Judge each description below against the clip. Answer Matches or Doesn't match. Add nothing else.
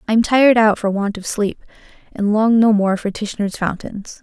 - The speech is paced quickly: Matches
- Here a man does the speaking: Doesn't match